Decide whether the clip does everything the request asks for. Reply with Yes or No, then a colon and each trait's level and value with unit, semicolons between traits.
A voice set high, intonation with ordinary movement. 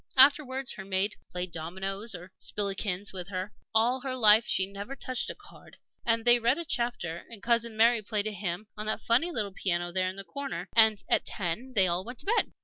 Yes: high, 210 Hz; average, 4.1 semitones